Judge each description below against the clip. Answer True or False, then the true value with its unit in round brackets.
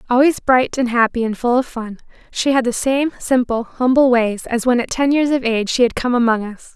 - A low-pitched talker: False (245 Hz)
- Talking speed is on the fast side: True (240 wpm)